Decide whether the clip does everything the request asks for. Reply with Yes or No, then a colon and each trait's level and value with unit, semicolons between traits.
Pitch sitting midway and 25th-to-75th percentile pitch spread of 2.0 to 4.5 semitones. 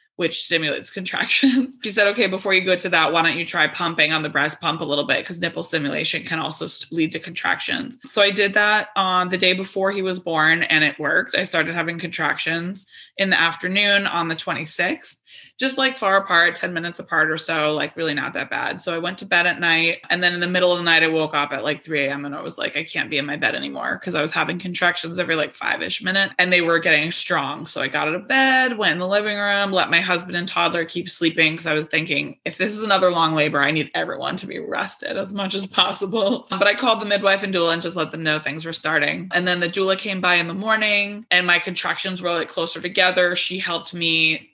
Yes: medium, 175 Hz; average, 3.1 semitones